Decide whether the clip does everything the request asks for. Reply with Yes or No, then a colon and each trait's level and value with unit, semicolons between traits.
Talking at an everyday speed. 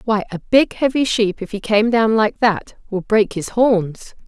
No: fast, 210 wpm